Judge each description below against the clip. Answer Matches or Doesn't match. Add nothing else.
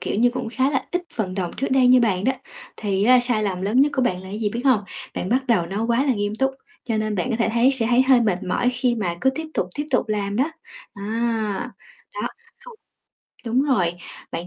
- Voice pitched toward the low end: Doesn't match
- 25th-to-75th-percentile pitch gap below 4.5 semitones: Matches